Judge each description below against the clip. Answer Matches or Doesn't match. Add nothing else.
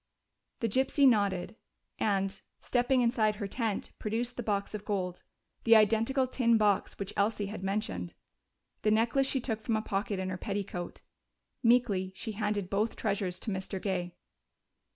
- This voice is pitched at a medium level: Doesn't match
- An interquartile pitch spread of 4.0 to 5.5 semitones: Doesn't match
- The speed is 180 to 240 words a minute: Doesn't match